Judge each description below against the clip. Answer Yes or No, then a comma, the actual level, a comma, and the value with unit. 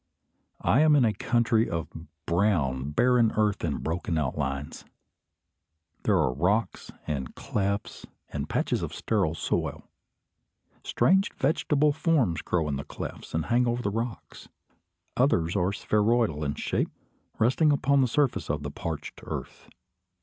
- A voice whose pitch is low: Yes, low, 100 Hz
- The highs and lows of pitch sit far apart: Yes, wide, 7.7 semitones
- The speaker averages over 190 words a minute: No, average, 140 wpm